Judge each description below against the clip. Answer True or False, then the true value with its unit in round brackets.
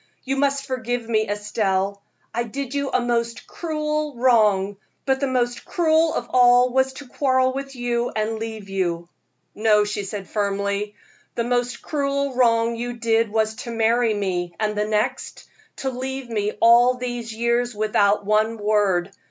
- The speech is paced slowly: False (160 wpm)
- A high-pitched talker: True (235 Hz)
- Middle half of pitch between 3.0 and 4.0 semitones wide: True (3.3 semitones)